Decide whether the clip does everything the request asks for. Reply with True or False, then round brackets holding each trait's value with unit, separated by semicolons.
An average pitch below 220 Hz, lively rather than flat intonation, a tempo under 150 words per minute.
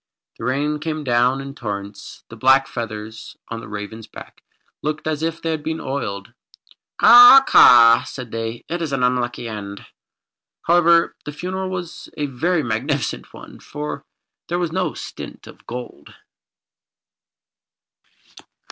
True (135 Hz; 5.7 semitones; 140 wpm)